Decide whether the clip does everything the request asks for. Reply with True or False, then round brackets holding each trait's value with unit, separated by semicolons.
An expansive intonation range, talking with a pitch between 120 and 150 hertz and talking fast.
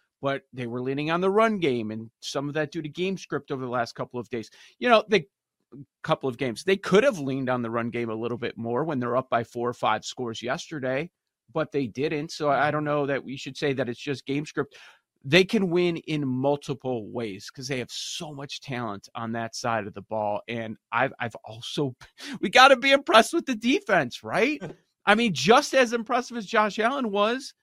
True (7.7 semitones; 140 Hz; 230 wpm)